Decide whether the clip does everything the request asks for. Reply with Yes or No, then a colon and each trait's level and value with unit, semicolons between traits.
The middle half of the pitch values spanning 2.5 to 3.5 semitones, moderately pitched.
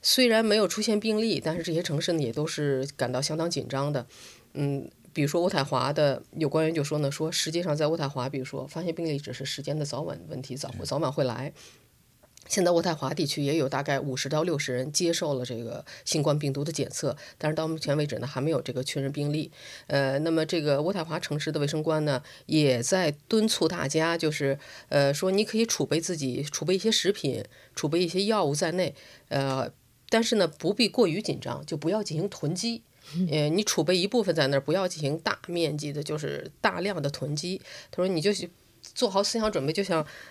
No: average, 4.3 semitones; medium, 155 Hz